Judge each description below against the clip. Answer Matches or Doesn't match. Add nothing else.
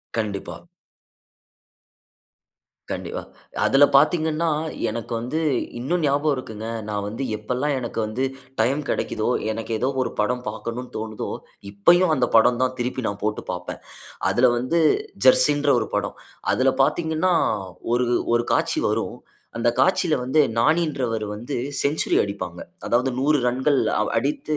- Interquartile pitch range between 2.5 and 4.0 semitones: Doesn't match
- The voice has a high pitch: Doesn't match